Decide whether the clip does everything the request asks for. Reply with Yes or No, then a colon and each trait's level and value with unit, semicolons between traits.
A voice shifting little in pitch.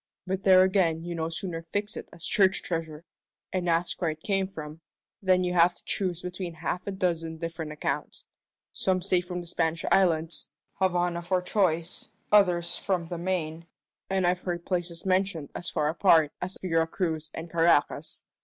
Yes: narrow, 2.2 semitones